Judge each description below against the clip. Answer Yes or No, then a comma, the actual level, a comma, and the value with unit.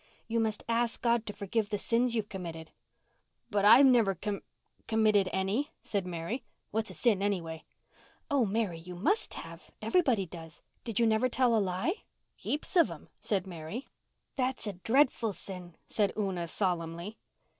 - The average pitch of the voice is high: Yes, high, 210 Hz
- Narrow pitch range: No, average, 4.2 semitones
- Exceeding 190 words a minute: No, average, 160 wpm